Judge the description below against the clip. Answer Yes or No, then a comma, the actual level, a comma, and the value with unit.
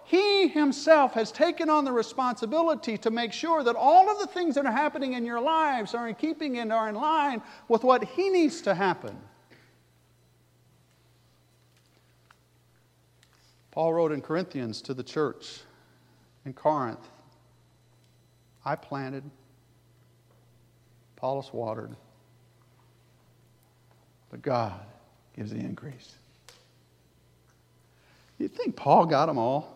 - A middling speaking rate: No, slow, 115 wpm